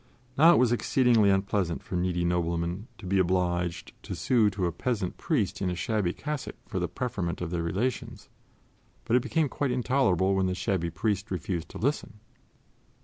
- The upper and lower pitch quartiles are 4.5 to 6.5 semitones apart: Yes, wide, 5.6 semitones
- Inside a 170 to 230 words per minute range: Yes, average, 180 wpm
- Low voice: Yes, very low, 95 Hz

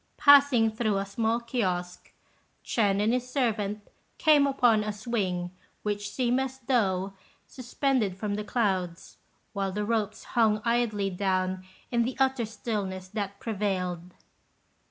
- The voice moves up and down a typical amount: Yes, average, 3.5 semitones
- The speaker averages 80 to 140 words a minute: Yes, slow, 135 wpm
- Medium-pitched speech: No, high, 210 Hz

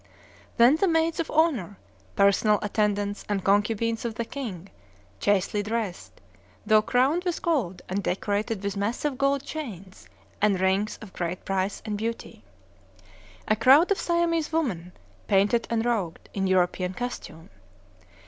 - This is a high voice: Yes, high, 215 Hz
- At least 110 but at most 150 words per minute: Yes, average, 140 wpm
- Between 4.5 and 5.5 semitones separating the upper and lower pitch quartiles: Yes, average, 4.9 semitones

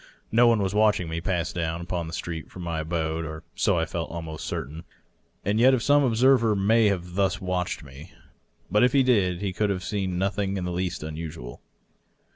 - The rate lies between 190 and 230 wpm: Yes, average, 200 wpm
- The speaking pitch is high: No, very low, 90 Hz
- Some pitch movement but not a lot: Yes, average, 4.1 semitones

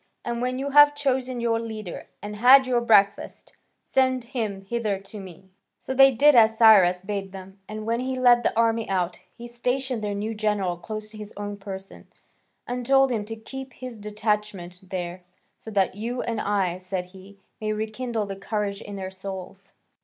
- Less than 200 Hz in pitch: No, high, 215 Hz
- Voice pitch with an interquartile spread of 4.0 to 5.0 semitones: No, average, 3.5 semitones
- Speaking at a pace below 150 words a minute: No, average, 185 wpm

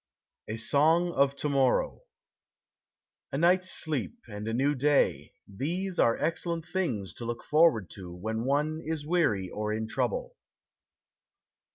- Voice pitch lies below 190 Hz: Yes, medium, 140 Hz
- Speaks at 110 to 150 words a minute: Yes, average, 140 wpm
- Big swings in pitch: Yes, wide, 6.8 semitones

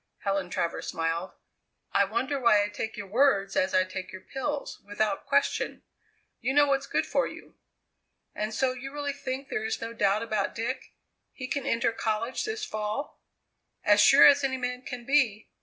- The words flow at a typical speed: Yes, average, 180 wpm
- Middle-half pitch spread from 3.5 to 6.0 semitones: Yes, average, 4.9 semitones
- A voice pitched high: Yes, high, 230 Hz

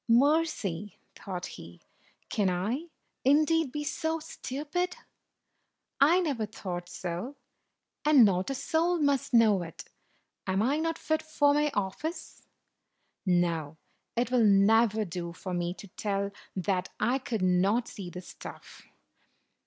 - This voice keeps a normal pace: No, slow, 130 wpm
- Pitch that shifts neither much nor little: No, wide, 8.0 semitones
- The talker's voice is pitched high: Yes, high, 220 Hz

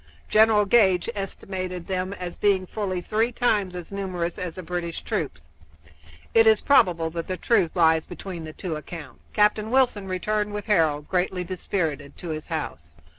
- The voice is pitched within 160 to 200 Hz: Yes, medium, 185 Hz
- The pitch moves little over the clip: No, average, 3.7 semitones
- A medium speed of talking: Yes, average, 165 wpm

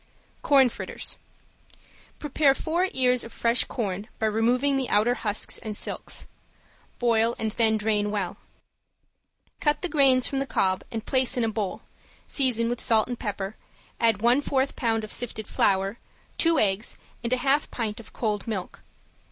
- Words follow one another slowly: No, average, 160 wpm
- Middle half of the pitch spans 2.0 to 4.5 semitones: Yes, average, 3.5 semitones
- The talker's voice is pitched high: Yes, high, 230 Hz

